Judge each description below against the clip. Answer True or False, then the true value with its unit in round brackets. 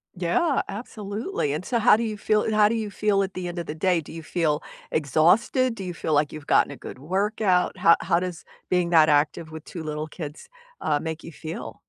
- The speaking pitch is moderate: True (175 Hz)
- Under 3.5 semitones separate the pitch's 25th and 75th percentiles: False (4.9 semitones)